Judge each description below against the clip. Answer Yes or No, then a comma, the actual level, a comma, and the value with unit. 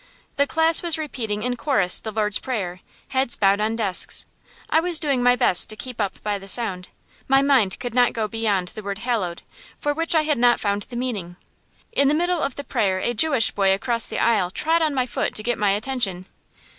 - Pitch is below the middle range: No, high, 235 Hz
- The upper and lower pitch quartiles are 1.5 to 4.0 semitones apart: No, average, 5.3 semitones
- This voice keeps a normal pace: No, fast, 220 wpm